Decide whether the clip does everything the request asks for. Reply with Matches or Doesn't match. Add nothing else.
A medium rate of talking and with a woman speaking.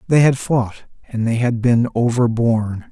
Doesn't match